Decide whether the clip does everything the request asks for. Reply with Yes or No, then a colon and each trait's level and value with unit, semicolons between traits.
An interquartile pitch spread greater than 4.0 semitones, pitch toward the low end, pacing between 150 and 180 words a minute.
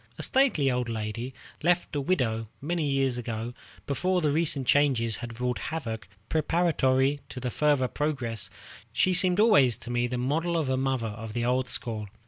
Yes: average, 4.5 semitones; low, 130 Hz; average, 170 wpm